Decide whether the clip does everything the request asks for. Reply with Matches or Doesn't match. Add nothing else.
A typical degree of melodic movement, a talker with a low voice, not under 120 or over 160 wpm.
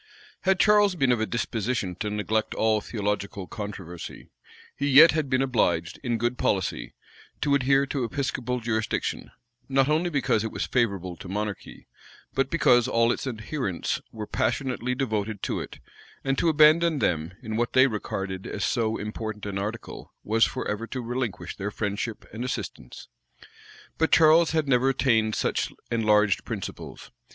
Matches